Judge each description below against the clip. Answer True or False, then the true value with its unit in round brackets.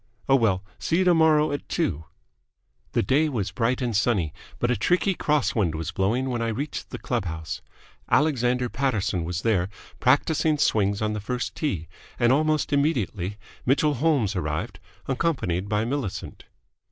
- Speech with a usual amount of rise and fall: False (6.9 semitones)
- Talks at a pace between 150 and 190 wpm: True (160 wpm)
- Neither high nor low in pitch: False (120 Hz)